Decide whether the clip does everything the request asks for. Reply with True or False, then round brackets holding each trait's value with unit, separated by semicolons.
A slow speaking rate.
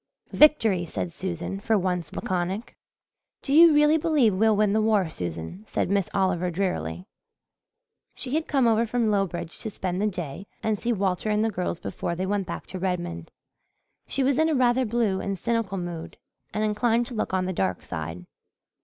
False (185 wpm)